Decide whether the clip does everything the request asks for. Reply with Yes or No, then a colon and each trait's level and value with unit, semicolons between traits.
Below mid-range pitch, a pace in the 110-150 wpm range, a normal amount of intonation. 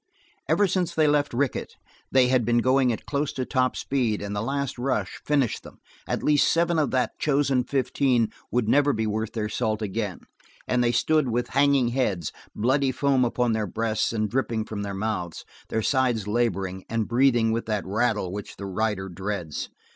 No: low, 120 Hz; average, 185 wpm; average, 4.0 semitones